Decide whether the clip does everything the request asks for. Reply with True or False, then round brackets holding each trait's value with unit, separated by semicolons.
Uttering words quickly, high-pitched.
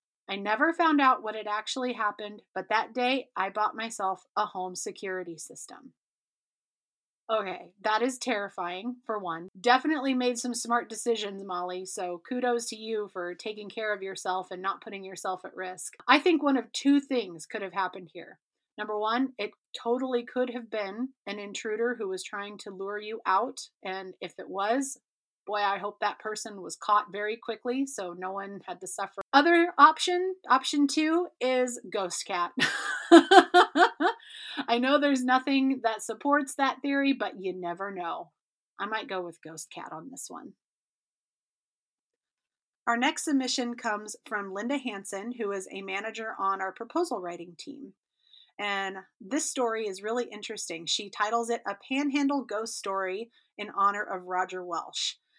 False (165 wpm; 215 Hz)